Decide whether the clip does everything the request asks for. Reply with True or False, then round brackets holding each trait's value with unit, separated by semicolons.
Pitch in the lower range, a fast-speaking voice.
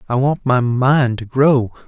False (130 Hz; 190 wpm)